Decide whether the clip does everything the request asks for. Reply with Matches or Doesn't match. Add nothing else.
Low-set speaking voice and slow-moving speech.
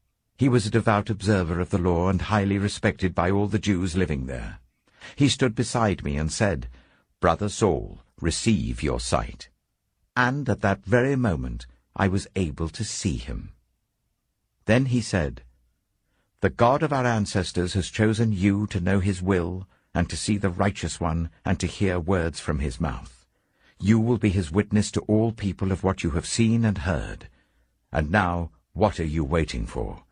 Doesn't match